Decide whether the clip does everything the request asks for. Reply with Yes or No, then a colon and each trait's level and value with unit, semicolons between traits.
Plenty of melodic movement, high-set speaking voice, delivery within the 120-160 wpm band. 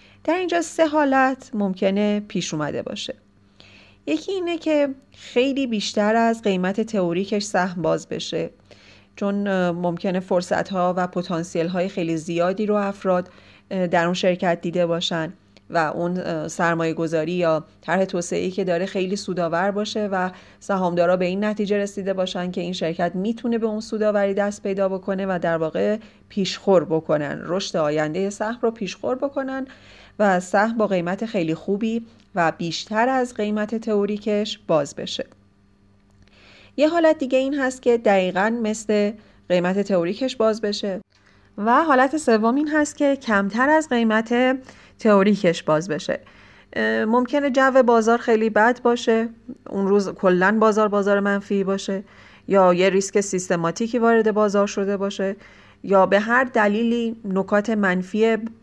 No: average, 4.0 semitones; high, 200 Hz; average, 140 wpm